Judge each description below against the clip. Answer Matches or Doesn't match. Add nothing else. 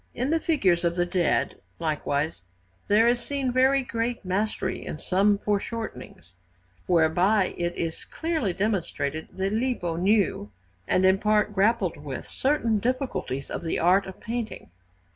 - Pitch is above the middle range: Matches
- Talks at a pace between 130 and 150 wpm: Matches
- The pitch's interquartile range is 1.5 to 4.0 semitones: Doesn't match